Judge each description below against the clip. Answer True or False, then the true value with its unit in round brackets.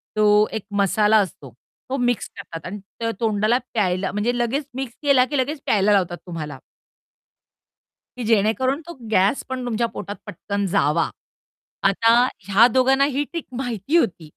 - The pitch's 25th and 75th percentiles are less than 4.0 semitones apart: False (4.6 semitones)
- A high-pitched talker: True (220 Hz)